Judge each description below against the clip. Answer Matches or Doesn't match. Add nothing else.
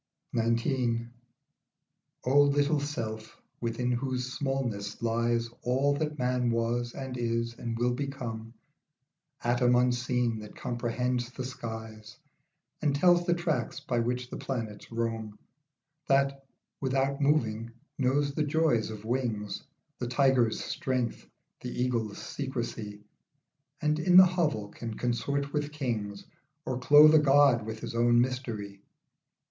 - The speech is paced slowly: Matches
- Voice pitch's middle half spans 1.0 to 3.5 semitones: Matches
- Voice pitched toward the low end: Matches